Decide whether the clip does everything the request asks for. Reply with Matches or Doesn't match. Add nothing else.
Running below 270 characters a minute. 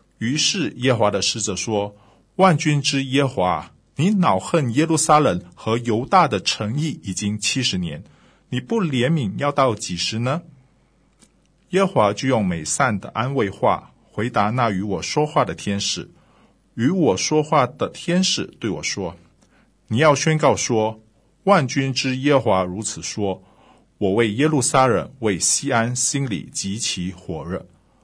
Matches